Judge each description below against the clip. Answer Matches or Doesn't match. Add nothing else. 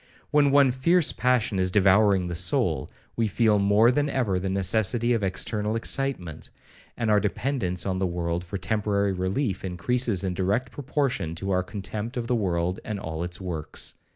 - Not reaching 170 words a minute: Doesn't match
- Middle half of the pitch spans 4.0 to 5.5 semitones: Matches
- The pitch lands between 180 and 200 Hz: Doesn't match